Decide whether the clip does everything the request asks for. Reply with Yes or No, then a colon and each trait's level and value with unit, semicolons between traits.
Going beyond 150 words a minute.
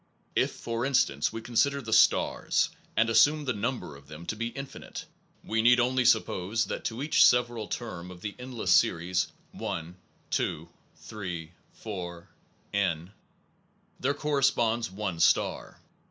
No: average, 145 wpm